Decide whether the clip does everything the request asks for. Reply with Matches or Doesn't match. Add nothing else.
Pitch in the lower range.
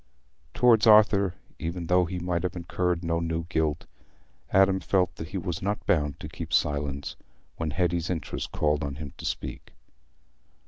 Matches